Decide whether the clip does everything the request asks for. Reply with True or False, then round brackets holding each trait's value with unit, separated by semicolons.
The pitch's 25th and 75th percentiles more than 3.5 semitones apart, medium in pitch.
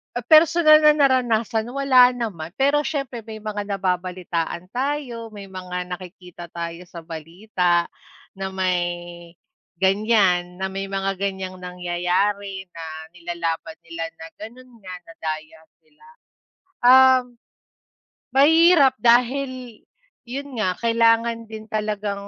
False (5.5 semitones; 205 Hz)